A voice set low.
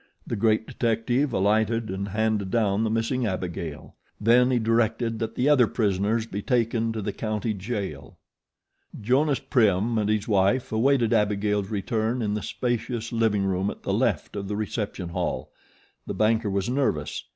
Yes: low, 110 Hz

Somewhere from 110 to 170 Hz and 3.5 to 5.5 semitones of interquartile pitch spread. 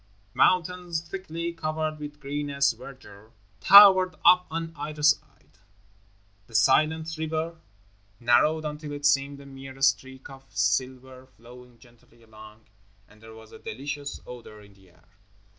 Yes: medium, 140 Hz; average, 4.8 semitones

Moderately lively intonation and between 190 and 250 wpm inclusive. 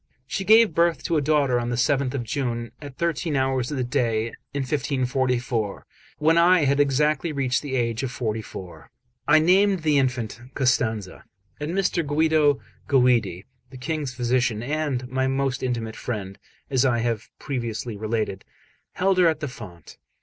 No: average, 4.1 semitones; average, 165 wpm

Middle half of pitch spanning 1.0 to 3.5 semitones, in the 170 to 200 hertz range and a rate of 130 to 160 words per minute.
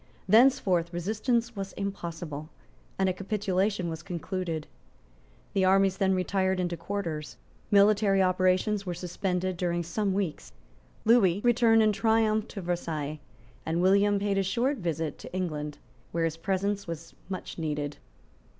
Yes: average, 3.0 semitones; high, 190 Hz; slow, 135 wpm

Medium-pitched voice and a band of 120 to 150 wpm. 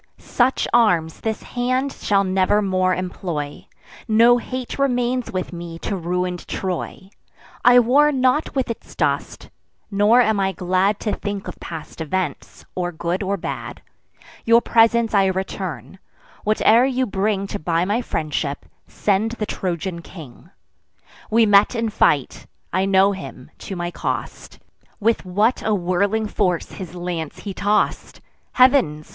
No: high, 195 Hz; average, 145 wpm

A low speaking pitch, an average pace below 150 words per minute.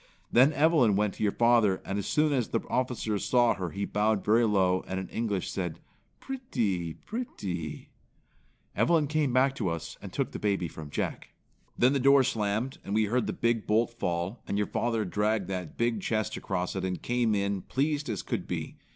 No: low, 110 Hz; average, 200 wpm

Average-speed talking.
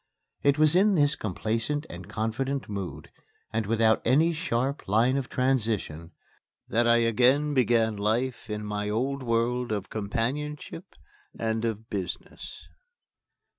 No: slow, 130 wpm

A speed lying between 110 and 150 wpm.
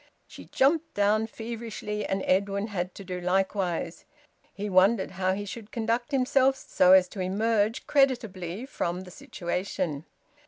Yes: average, 145 wpm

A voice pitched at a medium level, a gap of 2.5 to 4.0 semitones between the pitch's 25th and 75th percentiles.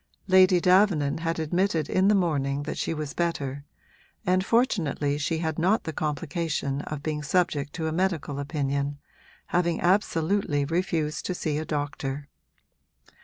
Yes: medium, 160 Hz; average, 3.7 semitones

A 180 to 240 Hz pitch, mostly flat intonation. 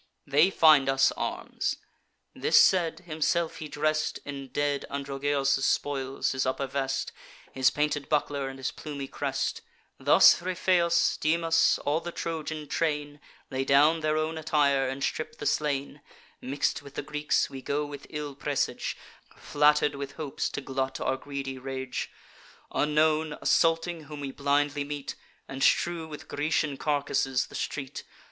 No: medium, 145 Hz; narrow, 2.2 semitones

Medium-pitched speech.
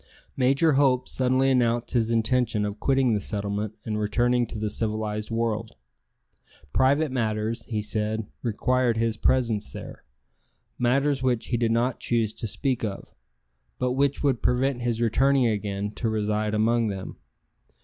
No: low, 115 Hz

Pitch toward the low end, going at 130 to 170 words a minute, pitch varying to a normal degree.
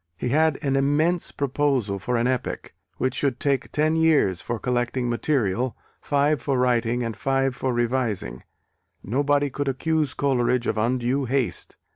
Yes: low, 130 Hz; average, 150 wpm; average, 3.0 semitones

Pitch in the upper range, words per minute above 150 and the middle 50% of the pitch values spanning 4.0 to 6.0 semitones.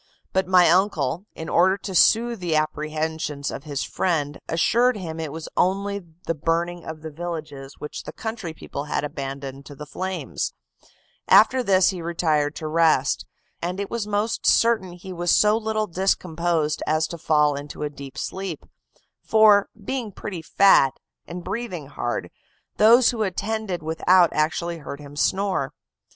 No: medium, 170 Hz; average, 160 wpm; average, 4.3 semitones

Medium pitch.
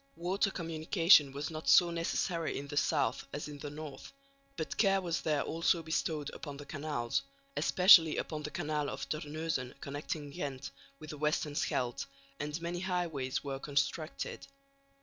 Yes: medium, 155 Hz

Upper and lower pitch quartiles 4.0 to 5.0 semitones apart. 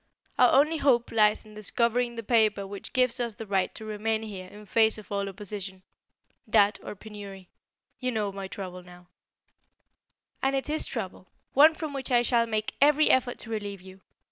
No: average, 3.5 semitones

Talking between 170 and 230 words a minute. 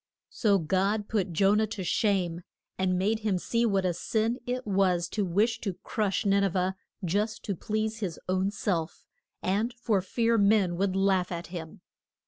Yes: average, 180 wpm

